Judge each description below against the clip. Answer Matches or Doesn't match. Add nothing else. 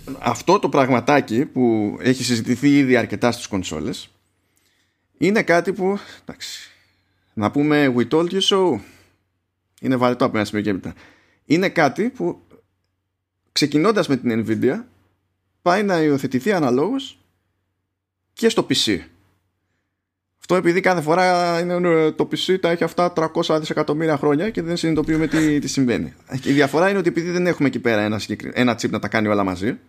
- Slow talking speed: Doesn't match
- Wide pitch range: Matches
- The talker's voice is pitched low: Matches